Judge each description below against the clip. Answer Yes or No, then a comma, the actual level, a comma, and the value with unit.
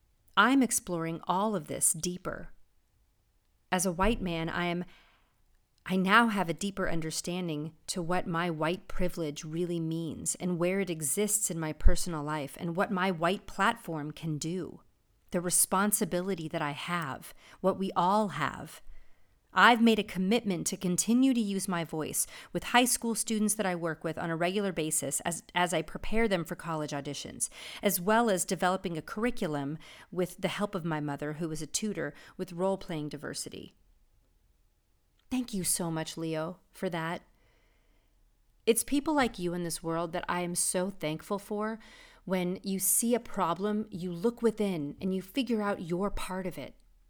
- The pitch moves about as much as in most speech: Yes, average, 3.6 semitones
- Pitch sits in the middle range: Yes, medium, 180 Hz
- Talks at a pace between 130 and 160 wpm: No, average, 170 wpm